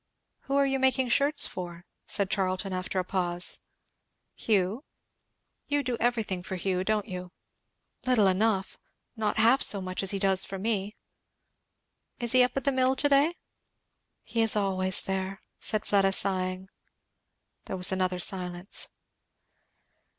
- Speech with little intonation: No, average, 4.3 semitones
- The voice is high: Yes, high, 195 Hz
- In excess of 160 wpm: No, average, 145 wpm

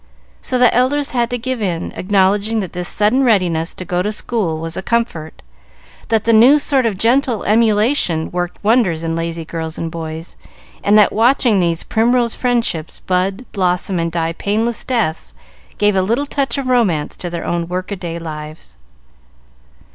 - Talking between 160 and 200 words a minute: Yes, average, 175 wpm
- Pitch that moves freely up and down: Yes, wide, 5.8 semitones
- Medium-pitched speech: No, high, 200 Hz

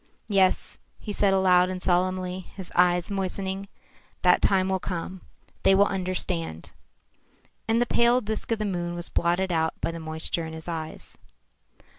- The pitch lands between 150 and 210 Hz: Yes, medium, 185 Hz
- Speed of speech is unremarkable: Yes, average, 160 wpm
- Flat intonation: Yes, narrow, 2.0 semitones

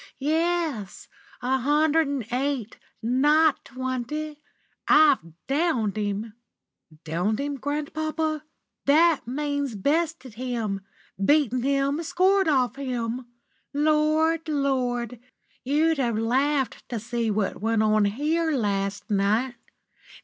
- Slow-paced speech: Yes, slow, 105 wpm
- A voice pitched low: No, very high, 270 Hz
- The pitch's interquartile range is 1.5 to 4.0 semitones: No, average, 4.8 semitones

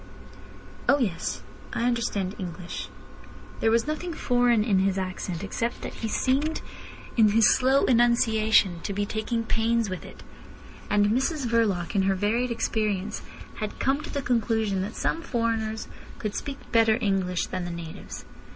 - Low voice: No, high, 220 Hz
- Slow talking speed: No, average, 155 wpm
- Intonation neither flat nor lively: Yes, average, 3.5 semitones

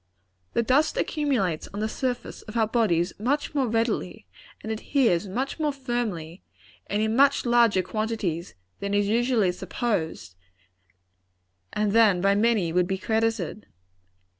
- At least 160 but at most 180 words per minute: No, average, 140 wpm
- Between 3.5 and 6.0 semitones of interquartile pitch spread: Yes, average, 4.1 semitones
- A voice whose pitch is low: No, high, 220 Hz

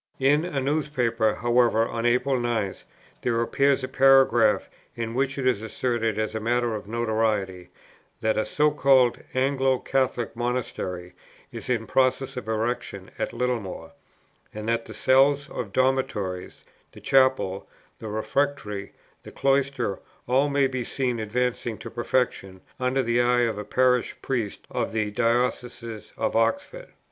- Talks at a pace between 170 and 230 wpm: No, average, 145 wpm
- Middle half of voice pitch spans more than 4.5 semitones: No, average, 3.2 semitones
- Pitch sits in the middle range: No, low, 120 Hz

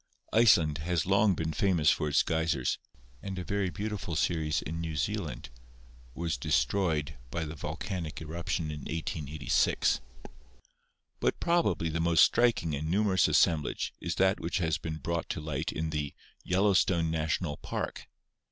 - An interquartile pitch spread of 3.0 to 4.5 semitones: Yes, average, 3.4 semitones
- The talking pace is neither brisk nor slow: Yes, average, 150 wpm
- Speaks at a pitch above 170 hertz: No, very low, 80 Hz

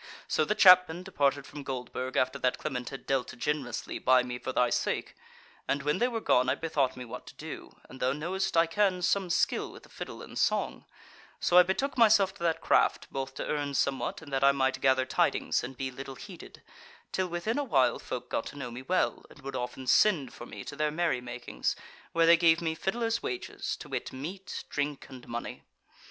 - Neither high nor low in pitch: Yes, medium, 145 Hz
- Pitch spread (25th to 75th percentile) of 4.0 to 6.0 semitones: Yes, wide, 5.4 semitones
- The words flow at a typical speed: No, fast, 210 wpm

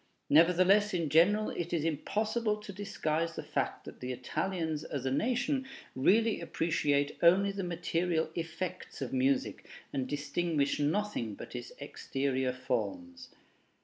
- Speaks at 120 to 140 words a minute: Yes, slow, 135 wpm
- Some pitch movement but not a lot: No, wide, 6.0 semitones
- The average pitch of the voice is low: No, medium, 165 Hz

